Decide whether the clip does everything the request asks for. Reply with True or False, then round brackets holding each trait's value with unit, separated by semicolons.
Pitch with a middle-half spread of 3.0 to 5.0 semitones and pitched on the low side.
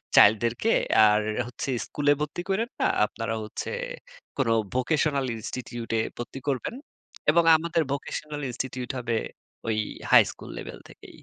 True (4.4 semitones; 130 Hz)